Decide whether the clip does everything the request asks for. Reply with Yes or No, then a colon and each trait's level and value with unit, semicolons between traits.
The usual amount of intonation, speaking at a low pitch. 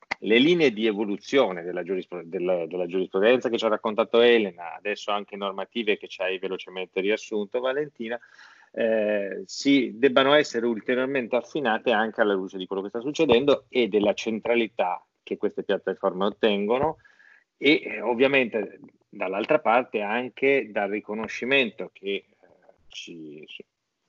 Yes: average, 4.0 semitones; low, 115 Hz